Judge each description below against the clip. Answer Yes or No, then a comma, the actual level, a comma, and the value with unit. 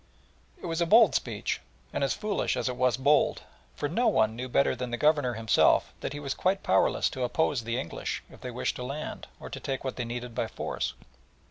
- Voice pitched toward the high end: No, low, 130 Hz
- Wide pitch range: No, average, 4.0 semitones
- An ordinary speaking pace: No, fast, 225 wpm